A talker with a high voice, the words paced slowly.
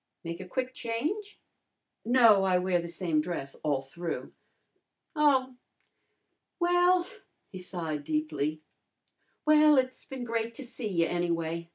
Yes: high, 205 Hz; slow, 130 wpm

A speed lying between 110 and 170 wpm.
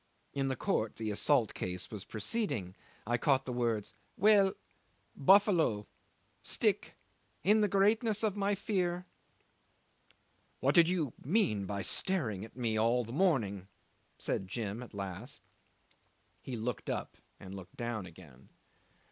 Yes: average, 140 wpm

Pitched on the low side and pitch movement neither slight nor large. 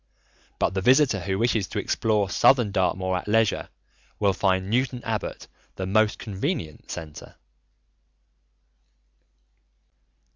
Yes: low, 100 Hz; average, 3.2 semitones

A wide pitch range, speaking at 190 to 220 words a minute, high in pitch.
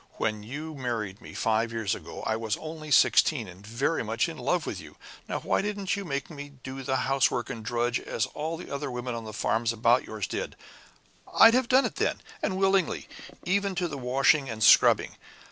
No: wide, 5.8 semitones; fast, 205 wpm; low, 130 Hz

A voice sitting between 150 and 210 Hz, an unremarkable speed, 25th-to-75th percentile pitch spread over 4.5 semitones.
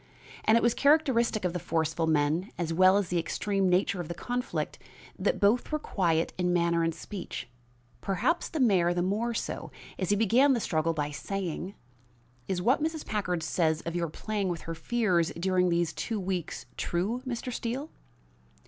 Yes: medium, 185 Hz; average, 180 wpm; average, 5.2 semitones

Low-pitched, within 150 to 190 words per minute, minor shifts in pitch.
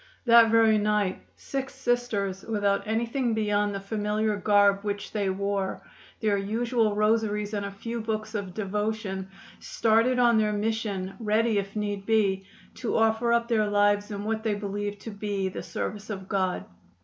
No: high, 210 Hz; average, 160 wpm; narrow, 1.8 semitones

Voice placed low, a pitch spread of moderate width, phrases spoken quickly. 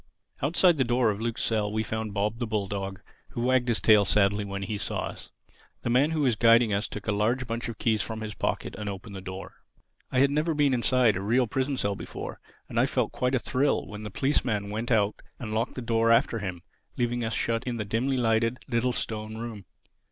Yes: low, 115 Hz; average, 3.0 semitones; fast, 225 wpm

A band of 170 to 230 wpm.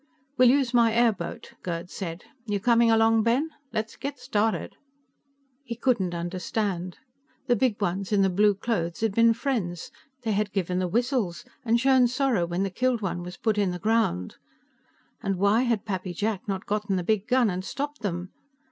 Yes: average, 180 wpm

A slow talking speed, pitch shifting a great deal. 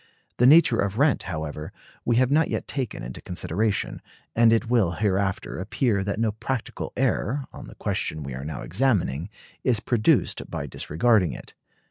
No: average, 165 wpm; wide, 5.7 semitones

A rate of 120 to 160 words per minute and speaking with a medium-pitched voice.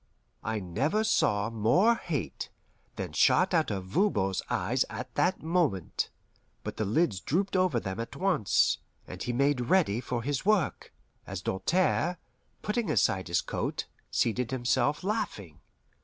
No: average, 140 wpm; low, 130 Hz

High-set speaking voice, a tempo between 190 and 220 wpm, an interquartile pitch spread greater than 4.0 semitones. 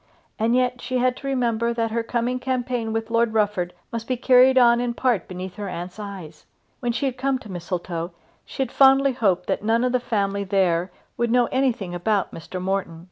Yes: high, 230 Hz; fast, 205 wpm; average, 4.5 semitones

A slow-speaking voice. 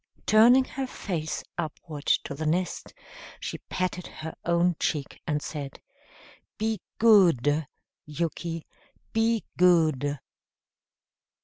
Yes: slow, 100 wpm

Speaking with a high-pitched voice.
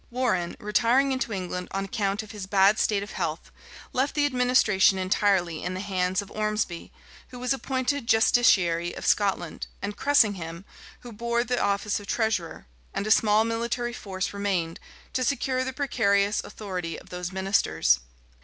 Yes: high, 205 Hz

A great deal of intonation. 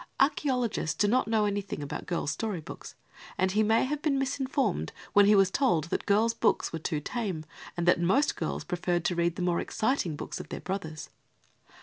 Yes: wide, 5.8 semitones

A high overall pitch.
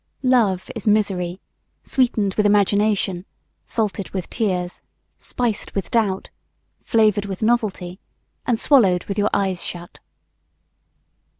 Yes: high, 205 Hz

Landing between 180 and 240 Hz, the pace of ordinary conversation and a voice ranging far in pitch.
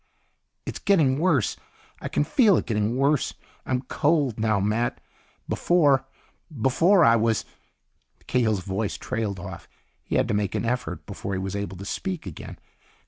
No: low, 120 Hz; average, 155 wpm; wide, 6.1 semitones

